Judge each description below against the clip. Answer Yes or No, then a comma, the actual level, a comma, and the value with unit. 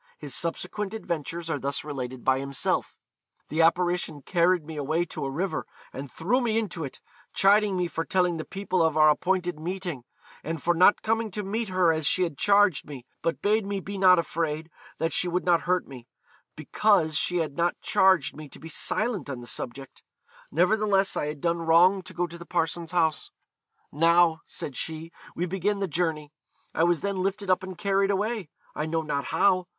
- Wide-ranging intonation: No, average, 3.5 semitones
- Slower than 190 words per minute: No, average, 195 wpm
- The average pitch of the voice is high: No, medium, 170 Hz